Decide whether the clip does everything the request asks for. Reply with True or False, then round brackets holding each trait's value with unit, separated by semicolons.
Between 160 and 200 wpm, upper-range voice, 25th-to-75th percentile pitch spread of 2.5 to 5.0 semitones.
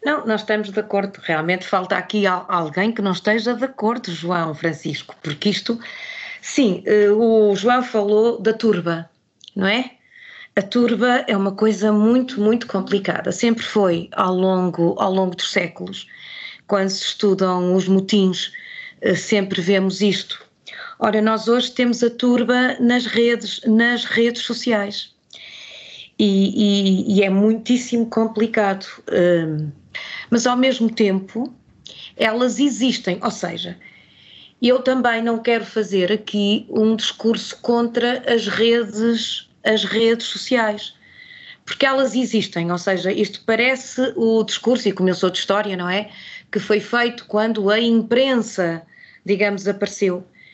False (135 wpm; 215 Hz; 3.5 semitones)